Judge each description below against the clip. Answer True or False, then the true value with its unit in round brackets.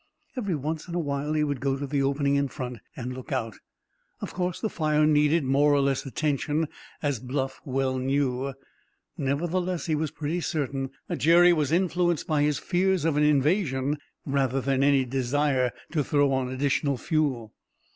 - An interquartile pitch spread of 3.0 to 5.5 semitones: False (2.6 semitones)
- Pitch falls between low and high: True (145 Hz)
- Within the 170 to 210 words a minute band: True (180 wpm)